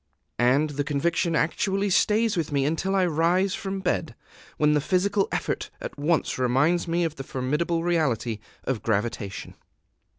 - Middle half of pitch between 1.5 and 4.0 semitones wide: No, average, 4.6 semitones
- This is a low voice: No, medium, 160 Hz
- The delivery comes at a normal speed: Yes, average, 155 wpm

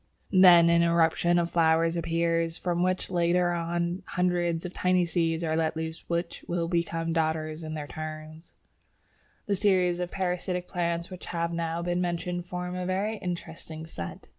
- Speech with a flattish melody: Yes, narrow, 1.4 semitones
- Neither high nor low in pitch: Yes, medium, 170 Hz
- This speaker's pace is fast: No, average, 165 wpm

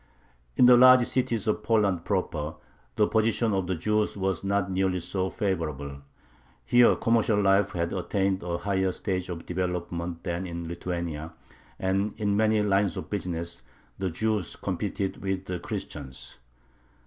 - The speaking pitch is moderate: No, very low, 95 Hz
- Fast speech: No, average, 150 wpm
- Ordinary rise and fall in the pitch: Yes, average, 3.2 semitones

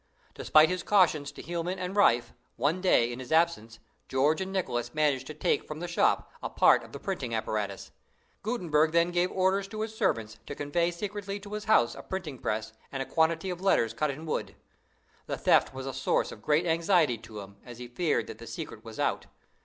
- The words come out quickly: Yes, fast, 210 wpm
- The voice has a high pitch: No, medium, 155 Hz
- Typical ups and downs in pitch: No, wide, 6.8 semitones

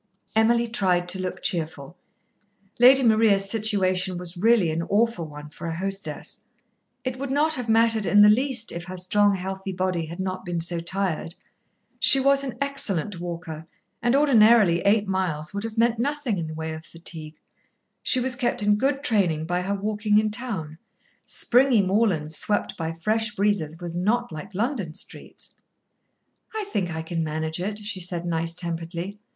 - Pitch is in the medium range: No, high, 195 Hz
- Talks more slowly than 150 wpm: No, average, 170 wpm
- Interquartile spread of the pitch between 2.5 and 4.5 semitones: No, average, 5.0 semitones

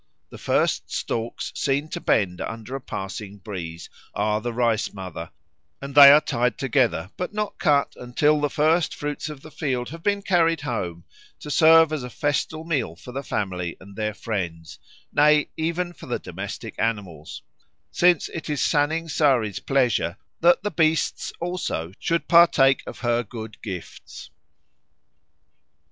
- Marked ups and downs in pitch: Yes, wide, 7.0 semitones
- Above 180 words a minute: No, average, 155 wpm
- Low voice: Yes, low, 130 Hz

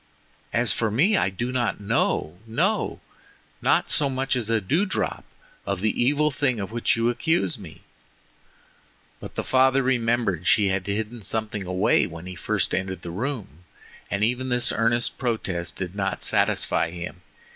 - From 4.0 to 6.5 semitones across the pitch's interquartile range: Yes, average, 4.9 semitones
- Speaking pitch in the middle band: No, low, 110 Hz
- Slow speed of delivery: No, average, 165 wpm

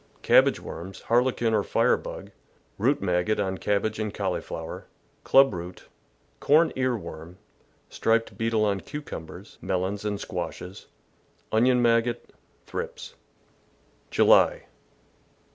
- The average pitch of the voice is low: Yes, low, 110 Hz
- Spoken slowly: Yes, slow, 115 wpm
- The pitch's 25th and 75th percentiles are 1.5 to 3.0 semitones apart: No, average, 4.5 semitones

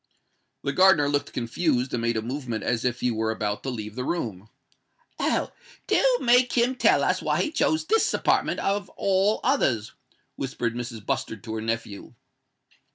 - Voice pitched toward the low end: Yes, low, 125 Hz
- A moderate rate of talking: Yes, average, 170 wpm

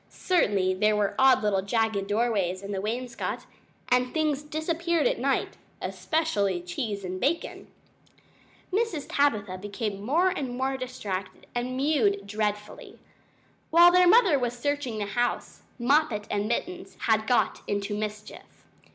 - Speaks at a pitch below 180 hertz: No, high, 235 Hz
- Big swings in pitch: Yes, wide, 6.0 semitones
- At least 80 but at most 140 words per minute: Yes, slow, 135 wpm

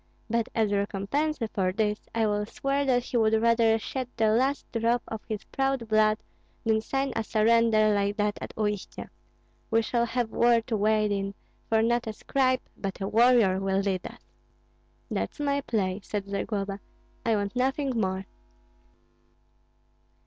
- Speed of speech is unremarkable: Yes, average, 160 wpm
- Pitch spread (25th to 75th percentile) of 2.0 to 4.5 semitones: Yes, narrow, 2.6 semitones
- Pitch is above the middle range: Yes, high, 220 Hz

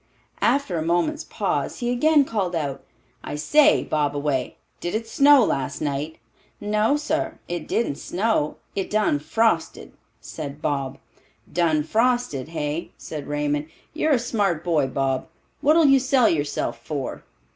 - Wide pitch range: Yes, wide, 8.7 semitones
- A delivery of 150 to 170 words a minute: No, average, 140 wpm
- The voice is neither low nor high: Yes, medium, 175 Hz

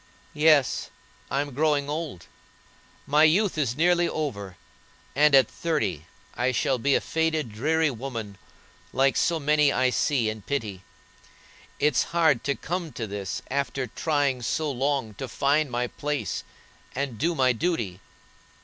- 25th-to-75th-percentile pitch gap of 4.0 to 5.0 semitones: Yes, average, 4.4 semitones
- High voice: No, medium, 140 Hz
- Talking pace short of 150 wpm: Yes, average, 140 wpm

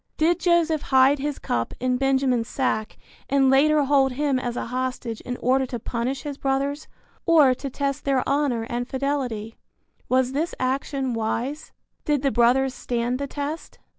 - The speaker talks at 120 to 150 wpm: No, average, 165 wpm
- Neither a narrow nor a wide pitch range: No, narrow, 2.3 semitones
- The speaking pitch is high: Yes, very high, 265 Hz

